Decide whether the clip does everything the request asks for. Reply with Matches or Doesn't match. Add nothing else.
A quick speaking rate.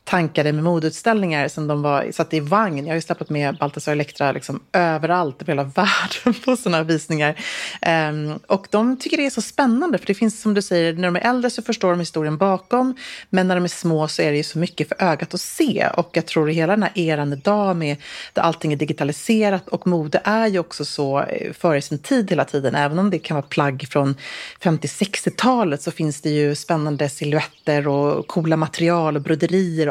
Matches